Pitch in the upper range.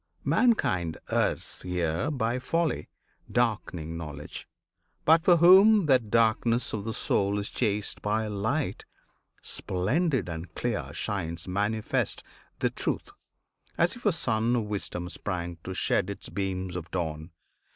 No: low, 105 Hz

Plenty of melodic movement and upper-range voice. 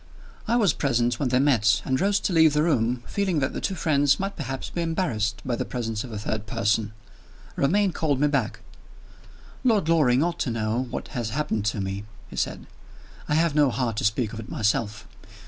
No: wide, 6.1 semitones; low, 130 Hz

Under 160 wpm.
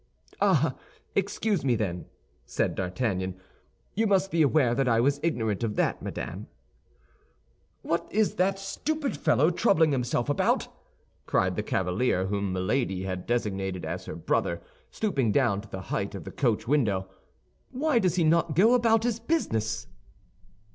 Yes: average, 150 wpm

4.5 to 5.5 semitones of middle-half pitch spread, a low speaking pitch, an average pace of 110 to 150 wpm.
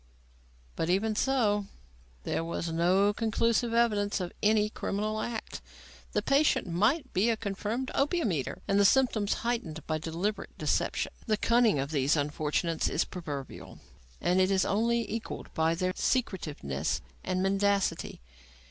No: average, 5.2 semitones; high, 200 Hz; average, 140 wpm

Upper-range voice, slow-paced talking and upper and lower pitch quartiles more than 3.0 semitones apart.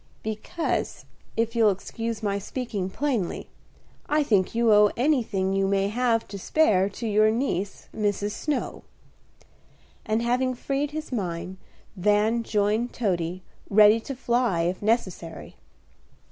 Yes: high, 215 Hz; slow, 130 wpm; average, 3.6 semitones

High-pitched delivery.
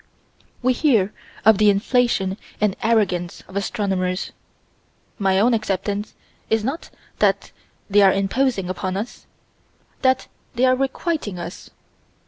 Yes: high, 205 Hz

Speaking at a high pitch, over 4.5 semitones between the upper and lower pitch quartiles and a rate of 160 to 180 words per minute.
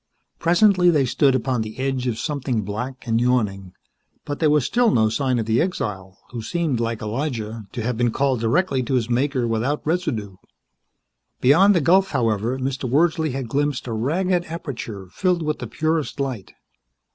No: low, 130 Hz; average, 5.1 semitones; average, 175 wpm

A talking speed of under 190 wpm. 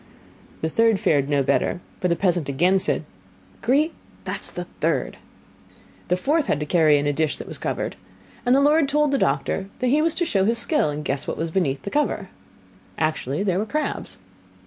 No: fast, 205 wpm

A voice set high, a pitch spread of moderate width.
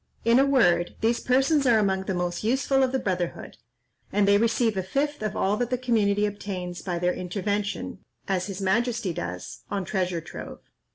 Yes: high, 205 Hz; average, 4.6 semitones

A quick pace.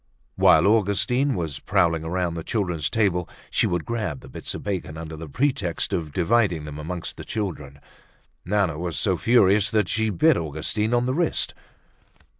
No: average, 170 wpm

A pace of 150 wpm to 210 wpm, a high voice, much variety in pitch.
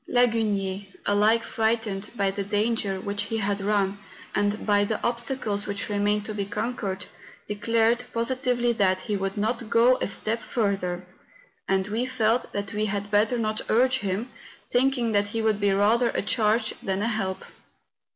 No: average, 170 wpm; high, 210 Hz; narrow, 2.4 semitones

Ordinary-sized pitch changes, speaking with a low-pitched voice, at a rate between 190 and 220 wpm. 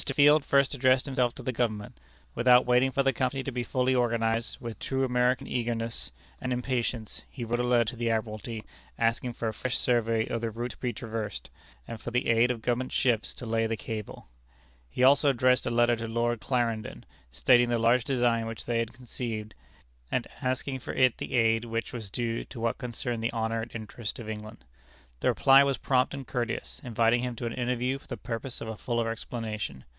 No: narrow, 1.8 semitones; low, 120 Hz; fast, 205 wpm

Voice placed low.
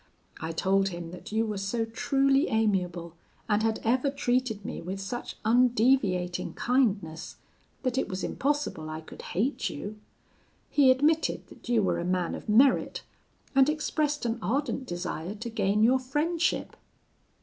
No: high, 225 Hz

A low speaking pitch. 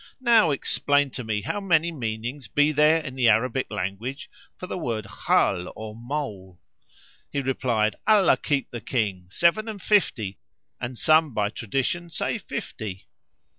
Yes: low, 130 Hz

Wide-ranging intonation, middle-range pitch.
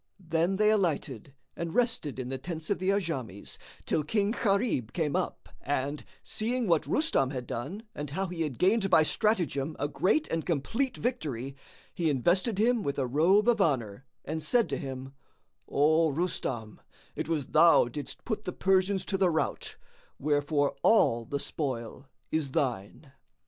Yes: wide, 6.1 semitones; medium, 160 Hz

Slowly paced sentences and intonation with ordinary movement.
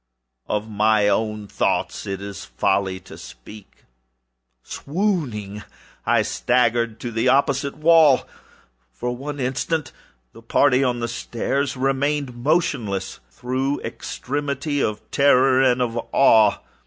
Yes: slow, 115 wpm; average, 4.4 semitones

